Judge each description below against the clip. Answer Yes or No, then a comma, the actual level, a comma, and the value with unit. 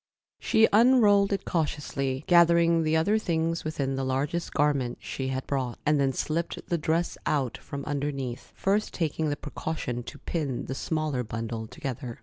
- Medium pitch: Yes, medium, 150 Hz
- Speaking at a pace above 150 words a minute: Yes, average, 160 wpm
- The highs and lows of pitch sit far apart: No, average, 4.0 semitones